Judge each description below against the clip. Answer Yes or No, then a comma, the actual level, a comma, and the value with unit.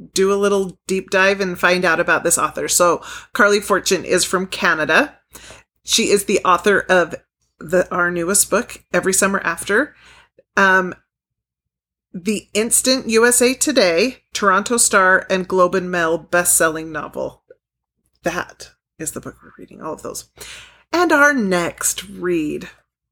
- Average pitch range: Yes, average, 4.1 semitones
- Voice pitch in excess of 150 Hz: Yes, high, 190 Hz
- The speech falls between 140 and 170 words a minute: Yes, average, 145 wpm